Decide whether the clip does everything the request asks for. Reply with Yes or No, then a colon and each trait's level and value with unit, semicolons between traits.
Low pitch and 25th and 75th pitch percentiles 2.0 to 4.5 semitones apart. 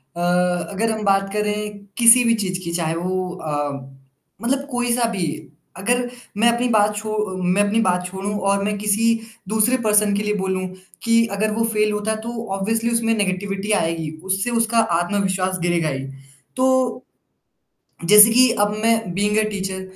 No: high, 210 Hz; average, 3.2 semitones